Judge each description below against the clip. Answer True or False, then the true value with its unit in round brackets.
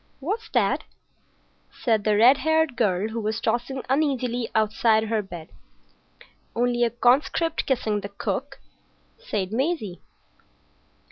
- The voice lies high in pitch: True (235 Hz)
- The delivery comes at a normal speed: False (120 wpm)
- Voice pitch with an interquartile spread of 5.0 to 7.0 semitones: False (4.0 semitones)